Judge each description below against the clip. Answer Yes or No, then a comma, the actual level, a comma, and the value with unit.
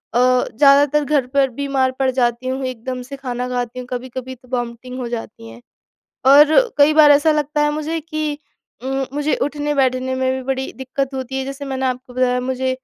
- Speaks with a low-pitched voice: No, very high, 260 Hz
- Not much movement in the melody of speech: Yes, narrow, 2.1 semitones